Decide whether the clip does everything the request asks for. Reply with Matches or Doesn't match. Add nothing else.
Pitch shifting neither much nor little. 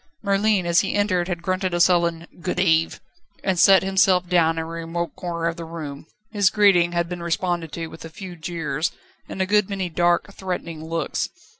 Doesn't match